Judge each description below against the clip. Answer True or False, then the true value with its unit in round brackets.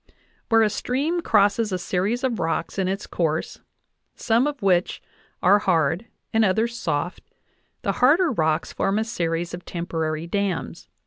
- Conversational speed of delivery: True (150 wpm)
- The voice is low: False (195 Hz)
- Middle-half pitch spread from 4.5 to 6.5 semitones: True (5.0 semitones)